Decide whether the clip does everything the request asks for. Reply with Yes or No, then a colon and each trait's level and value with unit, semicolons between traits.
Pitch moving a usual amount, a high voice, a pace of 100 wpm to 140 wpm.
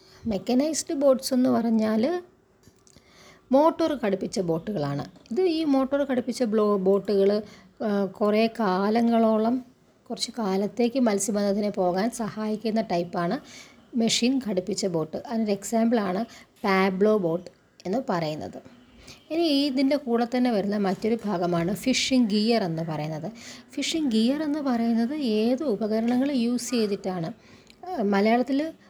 Yes: average, 4.1 semitones; high, 225 Hz; average, 105 wpm